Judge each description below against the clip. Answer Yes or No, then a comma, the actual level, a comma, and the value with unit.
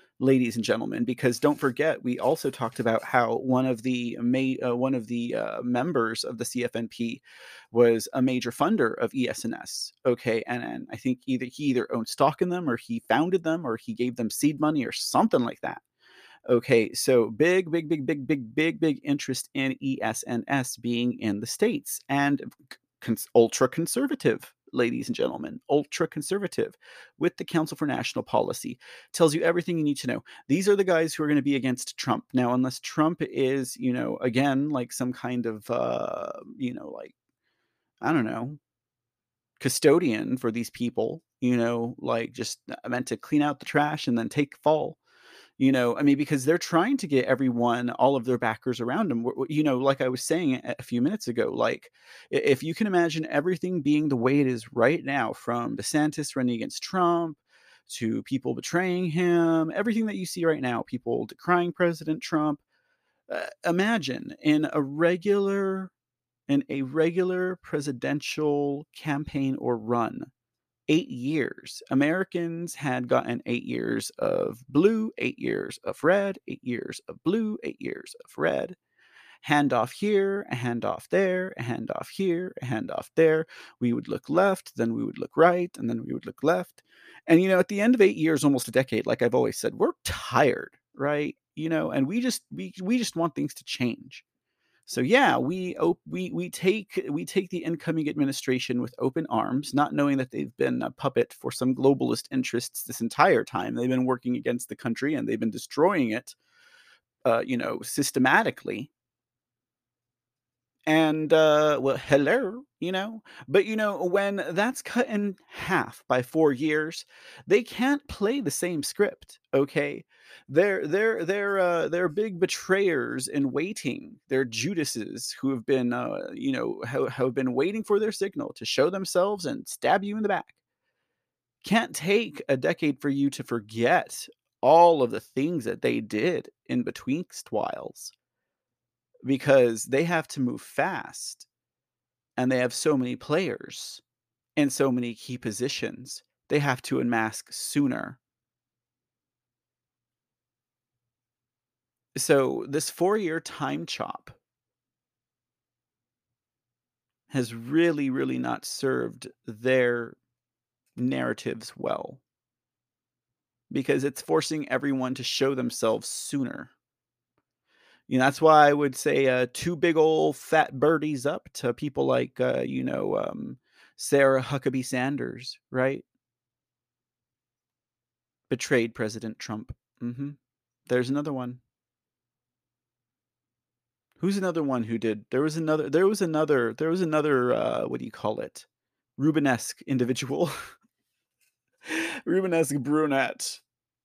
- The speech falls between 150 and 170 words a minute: Yes, average, 155 wpm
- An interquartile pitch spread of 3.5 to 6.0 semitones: Yes, average, 5.3 semitones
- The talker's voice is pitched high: No, medium, 140 Hz